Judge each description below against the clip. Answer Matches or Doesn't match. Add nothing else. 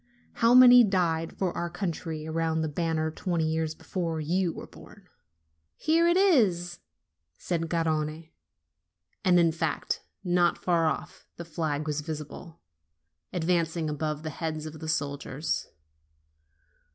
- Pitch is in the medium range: Matches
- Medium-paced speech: Doesn't match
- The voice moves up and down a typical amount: Doesn't match